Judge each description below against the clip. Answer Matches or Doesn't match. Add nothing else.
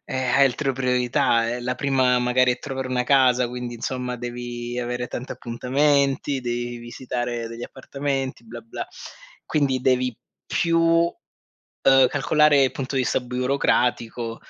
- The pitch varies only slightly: Matches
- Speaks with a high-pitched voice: Doesn't match